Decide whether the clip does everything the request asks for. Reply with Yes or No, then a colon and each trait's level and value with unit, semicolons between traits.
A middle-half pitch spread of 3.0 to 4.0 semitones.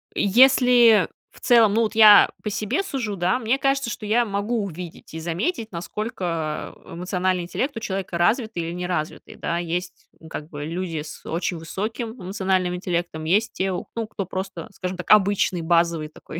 No: average, 4.4 semitones